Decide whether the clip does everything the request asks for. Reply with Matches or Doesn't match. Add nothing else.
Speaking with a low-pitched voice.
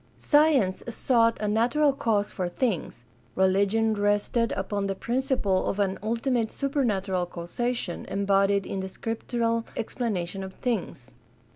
Doesn't match